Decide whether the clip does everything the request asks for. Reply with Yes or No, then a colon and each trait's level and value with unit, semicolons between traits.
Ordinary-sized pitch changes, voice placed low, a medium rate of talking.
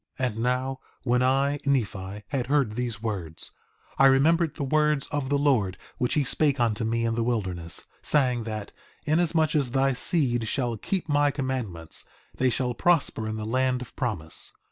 Yes: average, 4.1 semitones; low, 125 Hz; average, 175 wpm